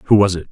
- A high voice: No, very low, 95 Hz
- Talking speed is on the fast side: Yes, fast, 350 wpm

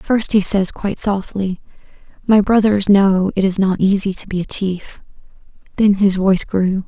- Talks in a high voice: Yes, high, 195 Hz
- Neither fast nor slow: Yes, average, 175 wpm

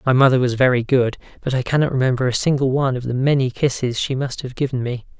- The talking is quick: Yes, fast, 240 wpm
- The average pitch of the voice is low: Yes, low, 130 Hz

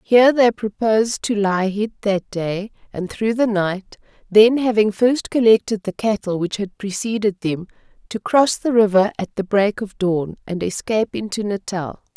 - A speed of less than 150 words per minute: No, average, 175 wpm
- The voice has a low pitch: No, high, 210 Hz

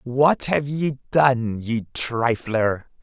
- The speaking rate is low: Yes, slow, 120 wpm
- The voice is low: Yes, low, 125 Hz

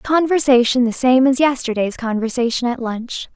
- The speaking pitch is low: No, very high, 250 Hz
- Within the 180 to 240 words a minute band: No, average, 145 wpm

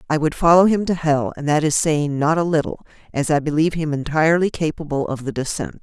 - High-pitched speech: No, medium, 155 Hz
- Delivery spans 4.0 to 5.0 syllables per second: No, 6.0 syllables/s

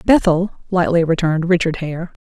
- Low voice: No, medium, 175 Hz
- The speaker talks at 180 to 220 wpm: No, slow, 135 wpm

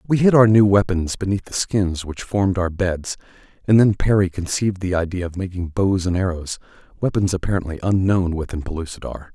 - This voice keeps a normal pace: Yes, average, 175 wpm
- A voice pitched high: No, very low, 95 Hz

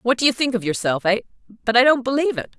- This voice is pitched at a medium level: No, high, 235 Hz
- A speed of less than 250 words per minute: No, fast, 255 wpm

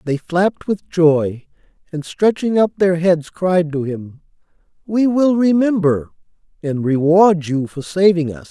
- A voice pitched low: No, medium, 170 Hz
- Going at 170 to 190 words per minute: No, average, 150 wpm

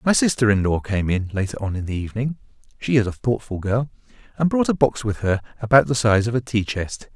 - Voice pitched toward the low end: Yes, low, 115 Hz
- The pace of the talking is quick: Yes, fast, 245 wpm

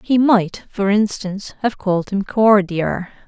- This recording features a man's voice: No, female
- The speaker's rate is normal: Yes, average, 145 wpm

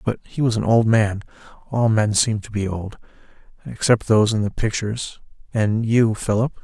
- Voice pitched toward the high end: No, low, 110 Hz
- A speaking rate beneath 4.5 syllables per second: No, 5.1 syllables/s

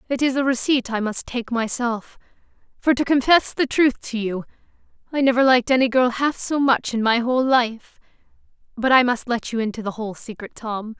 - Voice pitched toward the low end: No, high, 245 Hz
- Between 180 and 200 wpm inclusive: Yes, average, 195 wpm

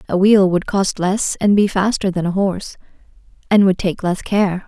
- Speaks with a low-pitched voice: No, high, 190 Hz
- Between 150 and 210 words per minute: Yes, fast, 205 wpm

